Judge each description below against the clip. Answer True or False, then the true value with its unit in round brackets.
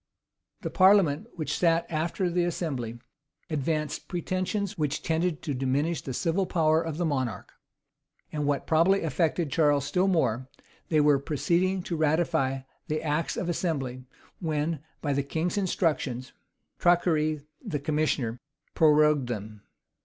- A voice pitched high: False (155 Hz)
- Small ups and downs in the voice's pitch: False (3.3 semitones)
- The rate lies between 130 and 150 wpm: True (135 wpm)